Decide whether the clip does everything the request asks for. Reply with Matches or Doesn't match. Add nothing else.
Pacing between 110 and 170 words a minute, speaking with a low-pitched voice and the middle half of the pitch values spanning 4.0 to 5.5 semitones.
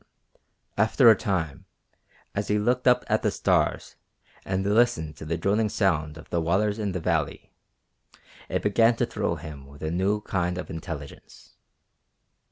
Matches